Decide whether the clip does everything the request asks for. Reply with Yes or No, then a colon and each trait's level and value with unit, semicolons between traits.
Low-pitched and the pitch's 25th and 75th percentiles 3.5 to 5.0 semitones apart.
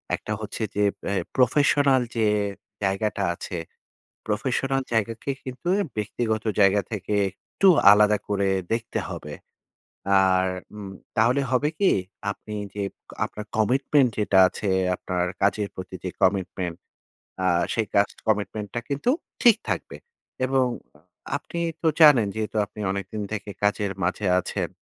Yes: low, 105 Hz; average, 4.0 semitones